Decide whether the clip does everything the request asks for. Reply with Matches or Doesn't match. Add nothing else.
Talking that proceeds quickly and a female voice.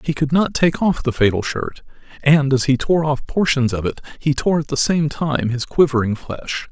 Doesn't match